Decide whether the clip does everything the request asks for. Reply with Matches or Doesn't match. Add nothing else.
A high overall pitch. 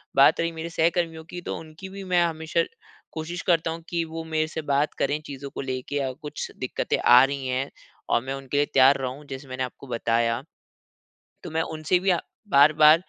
Doesn't match